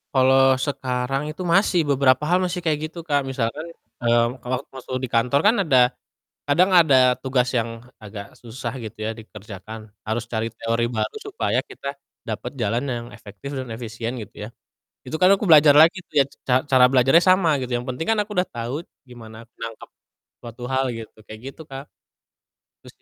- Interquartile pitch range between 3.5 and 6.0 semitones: Yes, average, 4.1 semitones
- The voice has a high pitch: No, low, 125 Hz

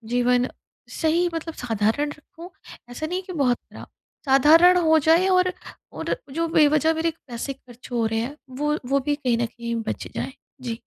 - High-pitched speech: Yes, very high, 290 Hz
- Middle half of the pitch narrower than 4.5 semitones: No, average, 5.0 semitones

